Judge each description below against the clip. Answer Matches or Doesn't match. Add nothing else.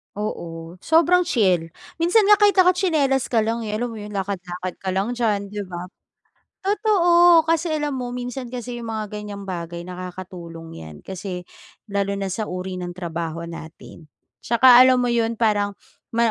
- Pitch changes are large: Matches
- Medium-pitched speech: Doesn't match